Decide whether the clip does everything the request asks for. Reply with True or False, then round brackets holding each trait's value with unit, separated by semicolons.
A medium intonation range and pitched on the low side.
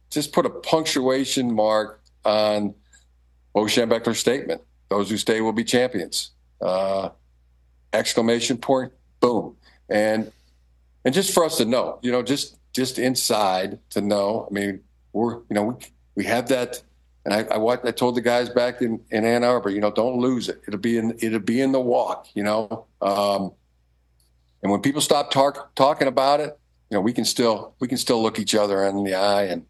True (4.7 semitones; 110 Hz)